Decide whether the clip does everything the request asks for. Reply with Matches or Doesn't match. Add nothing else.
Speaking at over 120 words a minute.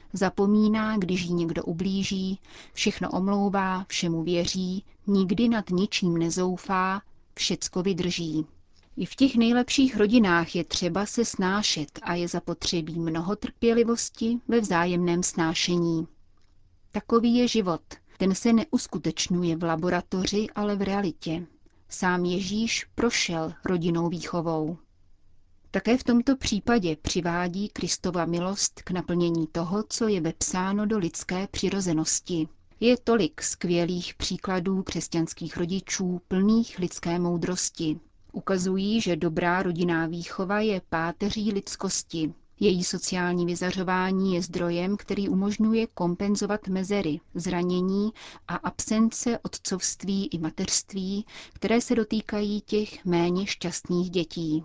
Doesn't match